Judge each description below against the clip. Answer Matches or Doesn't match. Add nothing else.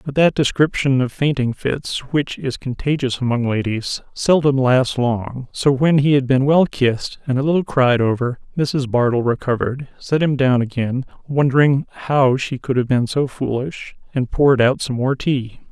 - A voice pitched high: Doesn't match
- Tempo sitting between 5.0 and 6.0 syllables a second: Doesn't match